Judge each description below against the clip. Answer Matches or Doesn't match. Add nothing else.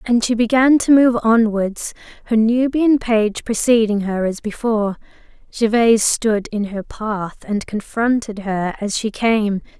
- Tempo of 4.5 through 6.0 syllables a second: Doesn't match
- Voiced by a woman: Matches